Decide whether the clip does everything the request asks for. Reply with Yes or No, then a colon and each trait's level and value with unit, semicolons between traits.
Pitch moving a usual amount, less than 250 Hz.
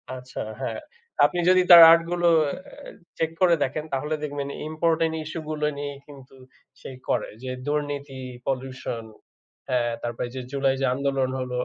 Yes: average, 3.1 semitones; medium, 140 Hz